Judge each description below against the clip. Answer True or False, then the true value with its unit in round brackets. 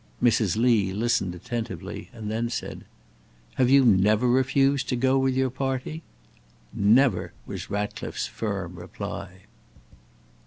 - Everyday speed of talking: False (120 wpm)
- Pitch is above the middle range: False (120 Hz)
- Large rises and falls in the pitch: False (4.3 semitones)